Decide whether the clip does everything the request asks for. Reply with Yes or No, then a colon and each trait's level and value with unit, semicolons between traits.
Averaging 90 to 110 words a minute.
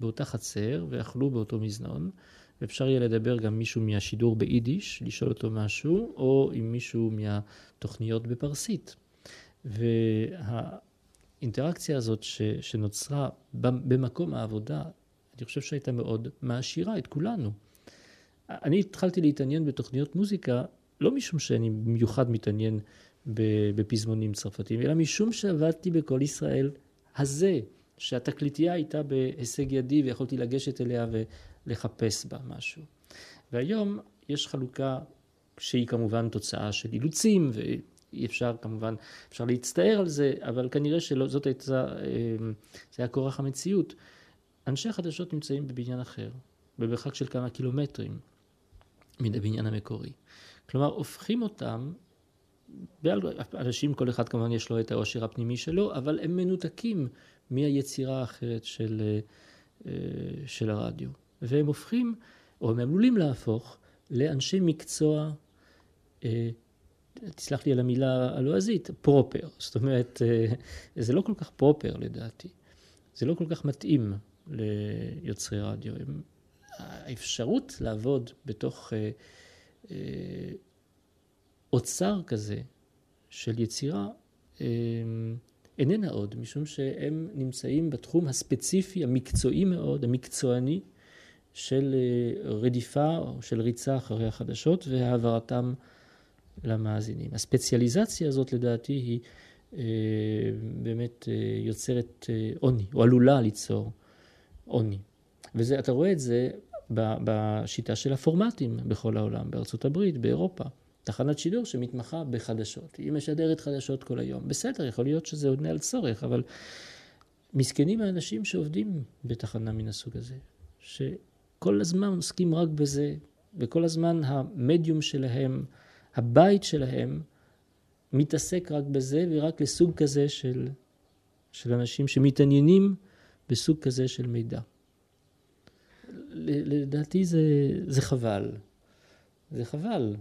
Yes: average, 105 wpm